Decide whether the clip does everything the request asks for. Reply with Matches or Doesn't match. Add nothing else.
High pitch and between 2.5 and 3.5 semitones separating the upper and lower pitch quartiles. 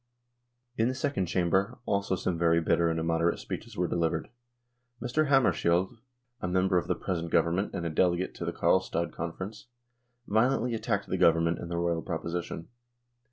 Doesn't match